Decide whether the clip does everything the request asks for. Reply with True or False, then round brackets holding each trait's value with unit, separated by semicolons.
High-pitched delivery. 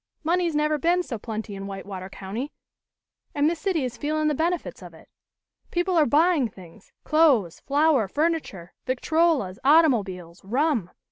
True (285 Hz)